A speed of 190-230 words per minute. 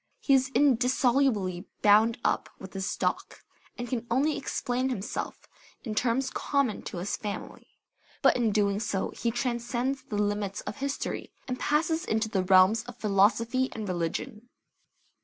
No: average, 150 wpm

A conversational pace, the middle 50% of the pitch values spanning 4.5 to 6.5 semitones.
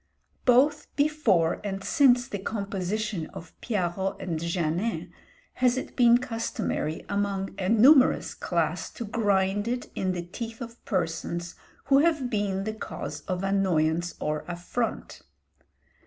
No: slow, 130 wpm; average, 5.0 semitones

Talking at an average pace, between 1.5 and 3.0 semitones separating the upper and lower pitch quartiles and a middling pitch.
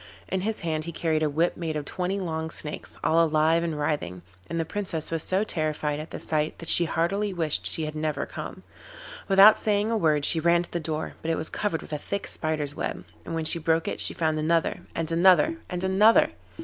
No: fast, 225 wpm; narrow, 2.5 semitones; medium, 165 Hz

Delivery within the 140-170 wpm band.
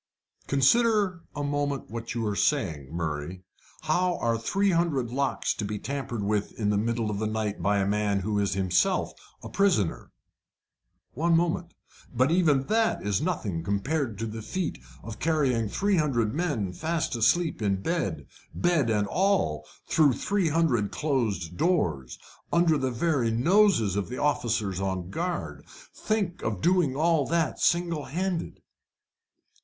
Yes: average, 150 wpm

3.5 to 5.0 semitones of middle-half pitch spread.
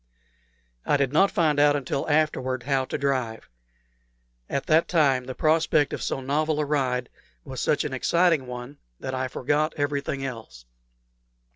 No: average, 2.8 semitones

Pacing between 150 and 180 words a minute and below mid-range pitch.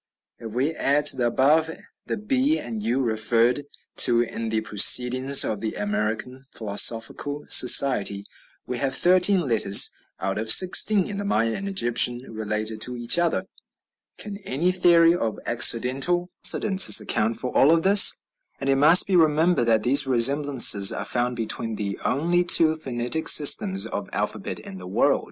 Yes: average, 160 wpm; low, 130 Hz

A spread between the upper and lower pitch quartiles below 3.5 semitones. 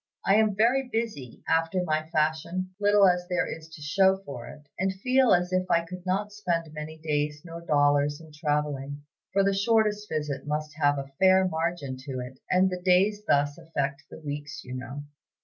No: average, 4.4 semitones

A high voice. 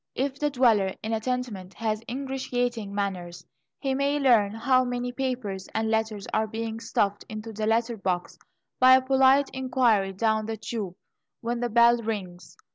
Yes: high, 225 Hz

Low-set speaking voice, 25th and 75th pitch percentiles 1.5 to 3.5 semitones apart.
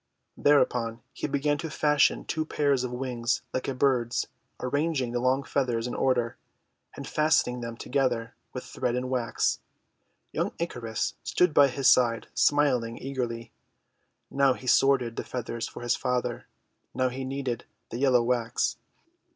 Yes: low, 125 Hz; narrow, 2.6 semitones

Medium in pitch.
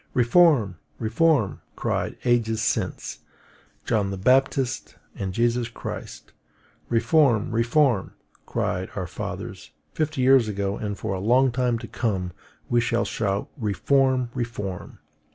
No: low, 115 Hz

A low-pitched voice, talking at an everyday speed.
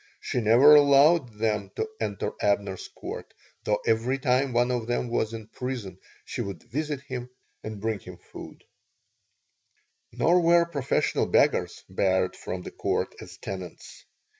Yes: low, 120 Hz; average, 145 wpm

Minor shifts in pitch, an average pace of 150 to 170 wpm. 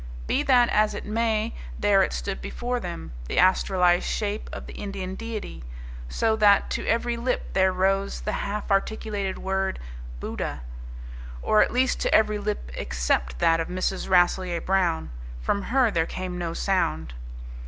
No: average, 3.4 semitones; average, 160 wpm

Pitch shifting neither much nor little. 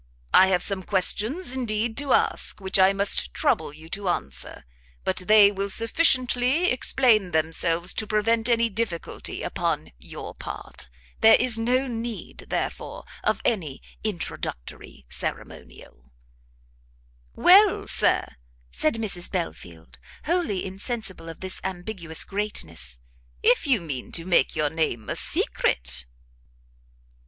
No: wide, 5.8 semitones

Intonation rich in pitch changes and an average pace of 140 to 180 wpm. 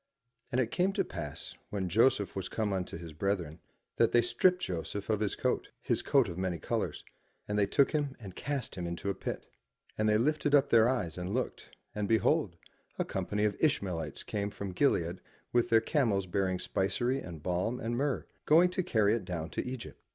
No: wide, 5.8 semitones; average, 200 wpm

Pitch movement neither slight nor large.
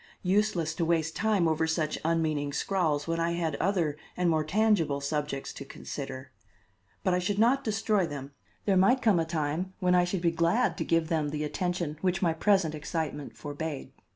Yes: average, 3.4 semitones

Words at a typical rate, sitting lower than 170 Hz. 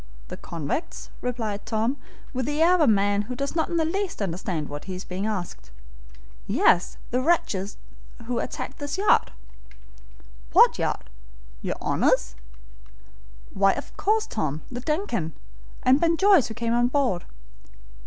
No: average, 155 wpm; high, 235 Hz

